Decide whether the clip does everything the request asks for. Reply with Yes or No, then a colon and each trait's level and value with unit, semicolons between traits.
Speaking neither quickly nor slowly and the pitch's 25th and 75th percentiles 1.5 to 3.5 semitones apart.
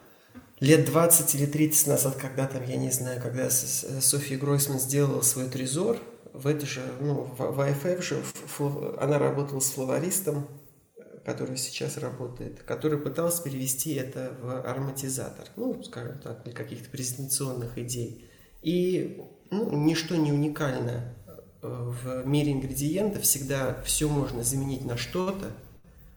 Yes: average, 130 wpm; average, 2.8 semitones